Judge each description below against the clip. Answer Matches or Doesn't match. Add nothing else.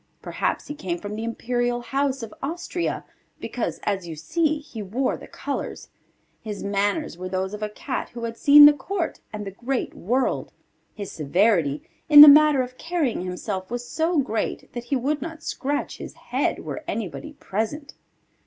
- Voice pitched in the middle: Doesn't match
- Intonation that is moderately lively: Doesn't match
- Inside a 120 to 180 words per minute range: Matches